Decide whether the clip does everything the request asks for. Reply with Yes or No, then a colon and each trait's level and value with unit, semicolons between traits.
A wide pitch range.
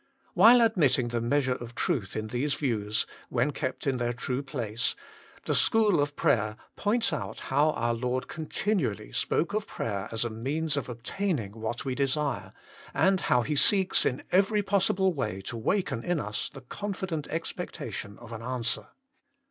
Yes: wide, 6.4 semitones